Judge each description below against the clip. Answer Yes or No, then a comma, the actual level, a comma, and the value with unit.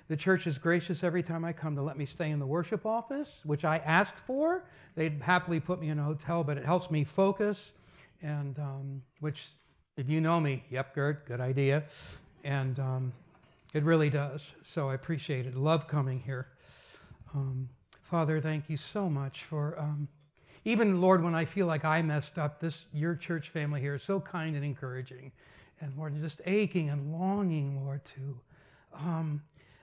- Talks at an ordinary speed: Yes, average, 185 wpm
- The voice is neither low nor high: Yes, medium, 150 Hz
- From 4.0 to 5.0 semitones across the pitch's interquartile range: No, average, 3.1 semitones